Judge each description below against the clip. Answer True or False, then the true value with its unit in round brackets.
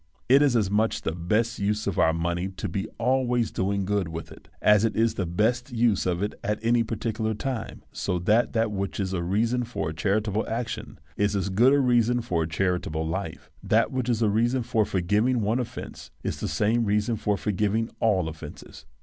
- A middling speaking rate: False (210 wpm)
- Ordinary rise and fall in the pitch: True (3.5 semitones)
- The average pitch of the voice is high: False (105 Hz)